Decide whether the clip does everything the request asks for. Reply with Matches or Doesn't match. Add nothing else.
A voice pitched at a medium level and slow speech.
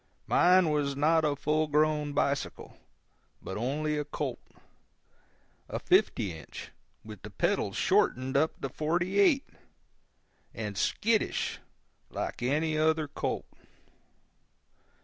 Matches